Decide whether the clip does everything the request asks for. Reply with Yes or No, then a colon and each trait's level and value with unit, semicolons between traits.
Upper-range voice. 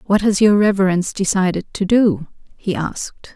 Yes: high, 195 Hz